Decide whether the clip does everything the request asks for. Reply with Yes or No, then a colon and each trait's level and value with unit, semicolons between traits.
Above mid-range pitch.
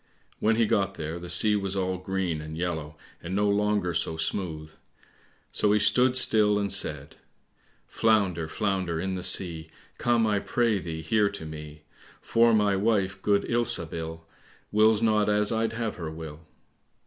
No: very low, 95 Hz